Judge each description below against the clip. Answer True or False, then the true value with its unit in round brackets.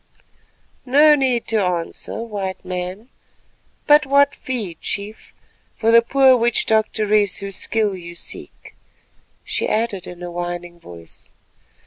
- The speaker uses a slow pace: True (125 wpm)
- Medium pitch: False (210 Hz)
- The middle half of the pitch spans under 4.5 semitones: False (4.8 semitones)